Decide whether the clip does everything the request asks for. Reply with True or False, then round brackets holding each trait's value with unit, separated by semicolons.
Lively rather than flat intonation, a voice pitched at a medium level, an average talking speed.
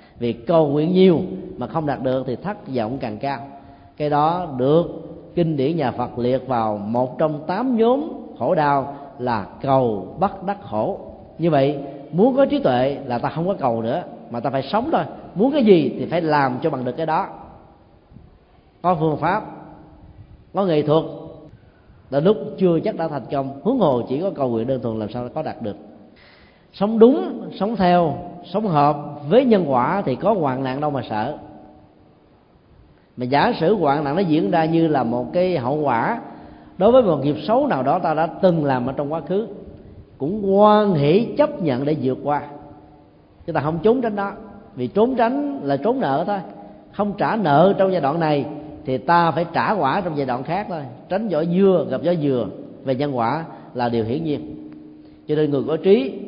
True (6.1 semitones; 150 Hz; 200 wpm)